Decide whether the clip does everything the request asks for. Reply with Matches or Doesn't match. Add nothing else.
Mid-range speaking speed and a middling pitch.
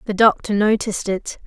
Doesn't match